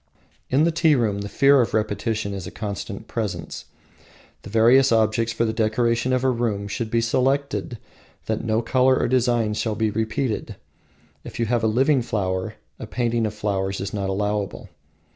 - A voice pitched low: Yes, low, 115 Hz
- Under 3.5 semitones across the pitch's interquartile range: Yes, average, 2.8 semitones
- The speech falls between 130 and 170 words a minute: No, average, 180 wpm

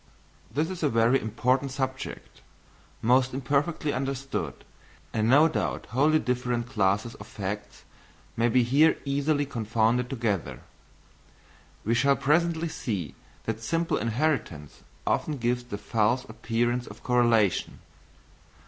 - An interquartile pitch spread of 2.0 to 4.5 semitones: Yes, average, 3.6 semitones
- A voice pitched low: Yes, low, 125 Hz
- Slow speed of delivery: Yes, slow, 120 wpm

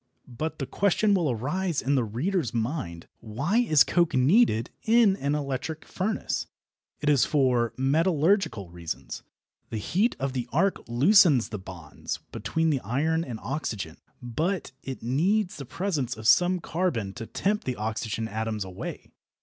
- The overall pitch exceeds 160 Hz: No, medium, 140 Hz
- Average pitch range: No, wide, 7.5 semitones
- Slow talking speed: No, average, 150 wpm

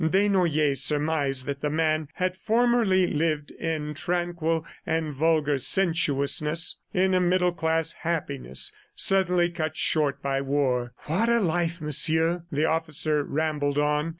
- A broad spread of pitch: No, average, 3.0 semitones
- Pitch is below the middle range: No, medium, 160 Hz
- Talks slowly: Yes, slow, 130 wpm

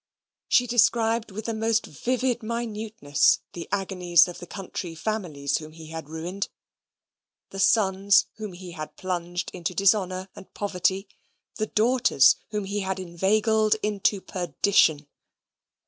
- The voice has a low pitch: No, high, 195 Hz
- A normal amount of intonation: Yes, average, 3.7 semitones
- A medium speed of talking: No, slow, 130 wpm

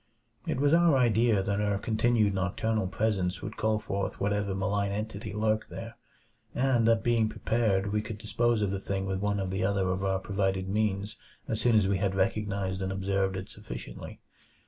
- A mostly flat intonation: Yes, narrow, 2.3 semitones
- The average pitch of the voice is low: Yes, low, 100 Hz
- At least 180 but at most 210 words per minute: Yes, average, 190 wpm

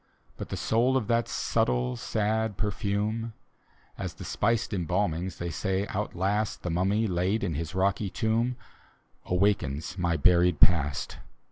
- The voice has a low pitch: Yes, very low, 95 Hz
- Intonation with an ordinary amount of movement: Yes, average, 3.9 semitones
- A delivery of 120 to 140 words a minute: Yes, slow, 135 wpm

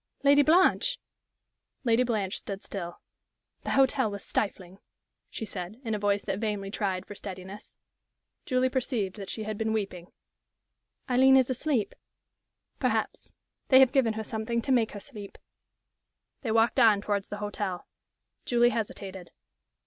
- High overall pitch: Yes, high, 215 Hz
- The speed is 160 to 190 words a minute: No, average, 145 wpm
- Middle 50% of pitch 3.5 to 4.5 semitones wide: Yes, average, 3.8 semitones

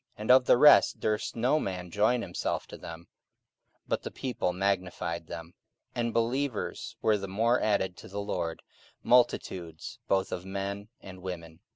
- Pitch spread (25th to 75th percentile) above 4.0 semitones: Yes, average, 4.6 semitones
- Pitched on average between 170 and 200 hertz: No, low, 100 Hz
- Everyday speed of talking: Yes, average, 170 wpm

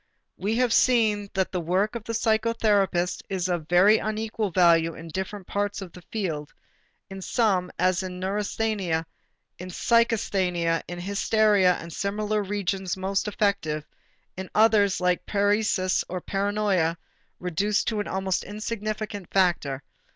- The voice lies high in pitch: Yes, high, 195 Hz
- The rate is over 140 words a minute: No, slow, 135 wpm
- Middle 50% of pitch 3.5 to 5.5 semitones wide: No, average, 2.8 semitones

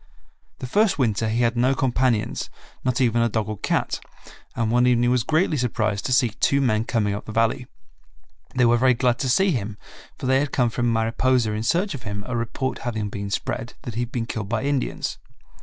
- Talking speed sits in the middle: No, fast, 215 wpm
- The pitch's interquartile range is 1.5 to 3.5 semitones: Yes, narrow, 2.5 semitones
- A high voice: No, low, 120 Hz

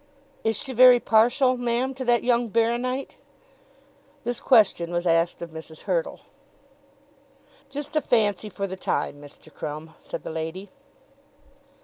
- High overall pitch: Yes, high, 225 Hz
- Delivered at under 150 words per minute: Yes, average, 140 wpm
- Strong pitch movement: Yes, wide, 6.5 semitones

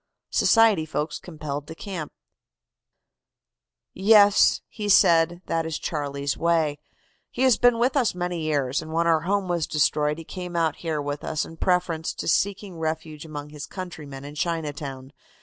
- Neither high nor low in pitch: Yes, medium, 165 Hz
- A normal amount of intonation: Yes, average, 3.3 semitones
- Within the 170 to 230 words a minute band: No, average, 160 wpm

